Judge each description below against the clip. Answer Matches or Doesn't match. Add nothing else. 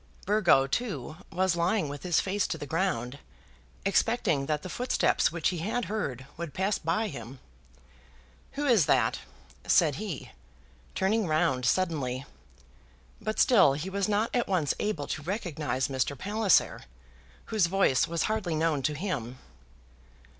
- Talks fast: Doesn't match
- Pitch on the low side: Doesn't match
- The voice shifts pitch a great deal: Matches